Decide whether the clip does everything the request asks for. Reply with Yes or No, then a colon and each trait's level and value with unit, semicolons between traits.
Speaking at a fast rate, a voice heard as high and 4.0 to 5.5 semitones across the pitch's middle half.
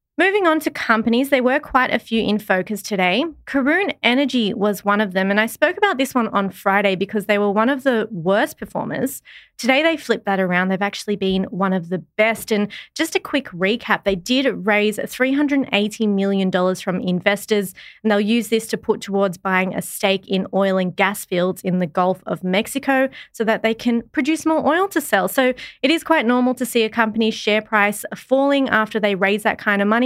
Yes: fast, 210 wpm; high, 215 Hz; average, 4.7 semitones